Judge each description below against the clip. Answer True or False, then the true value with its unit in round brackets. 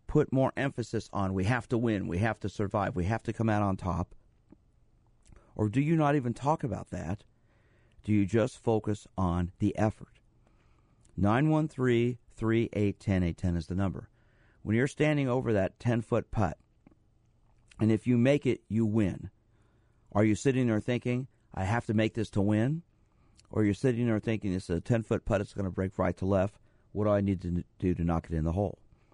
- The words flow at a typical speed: False (210 wpm)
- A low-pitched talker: True (110 Hz)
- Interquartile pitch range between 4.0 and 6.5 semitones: False (3.2 semitones)